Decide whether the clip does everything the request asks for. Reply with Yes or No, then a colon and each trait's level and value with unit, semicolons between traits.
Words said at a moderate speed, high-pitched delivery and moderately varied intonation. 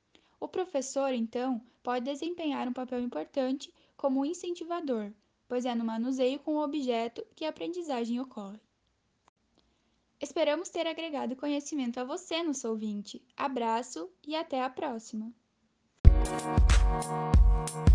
No: slow, 115 wpm; very high, 255 Hz; average, 4.9 semitones